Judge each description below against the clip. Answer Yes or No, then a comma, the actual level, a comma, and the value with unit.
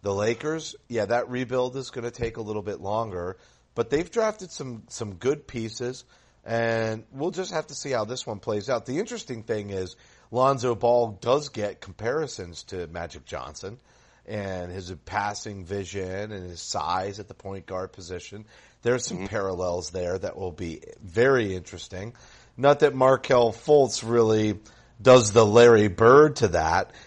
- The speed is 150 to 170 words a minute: Yes, average, 165 wpm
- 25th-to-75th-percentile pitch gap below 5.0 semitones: Yes, average, 4.6 semitones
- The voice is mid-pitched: No, low, 115 Hz